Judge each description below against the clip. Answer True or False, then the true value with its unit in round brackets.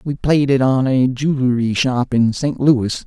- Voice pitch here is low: True (130 Hz)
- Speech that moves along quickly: False (195 wpm)